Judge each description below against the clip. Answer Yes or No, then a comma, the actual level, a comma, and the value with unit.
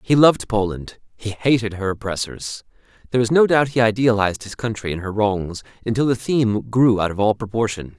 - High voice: No, low, 110 Hz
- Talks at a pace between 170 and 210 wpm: Yes, average, 195 wpm